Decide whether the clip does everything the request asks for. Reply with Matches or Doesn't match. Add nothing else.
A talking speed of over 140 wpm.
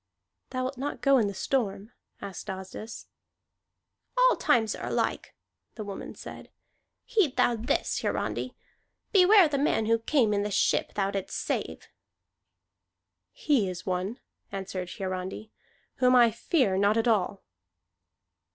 Doesn't match